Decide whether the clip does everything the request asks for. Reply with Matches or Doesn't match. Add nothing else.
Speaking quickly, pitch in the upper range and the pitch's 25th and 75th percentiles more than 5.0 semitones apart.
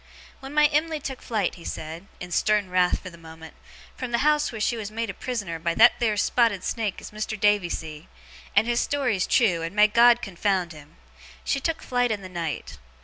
Matches